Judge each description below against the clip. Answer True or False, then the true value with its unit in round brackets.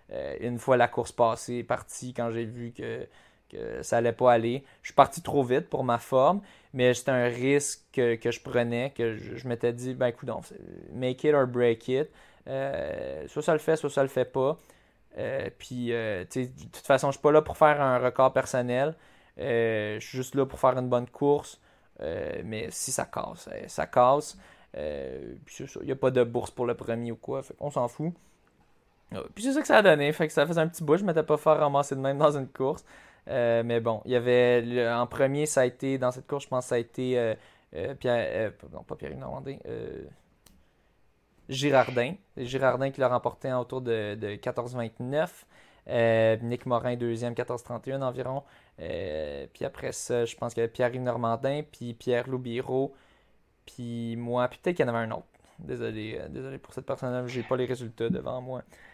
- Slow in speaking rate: False (215 wpm)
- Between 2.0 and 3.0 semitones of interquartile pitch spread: True (2.5 semitones)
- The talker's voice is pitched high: False (125 Hz)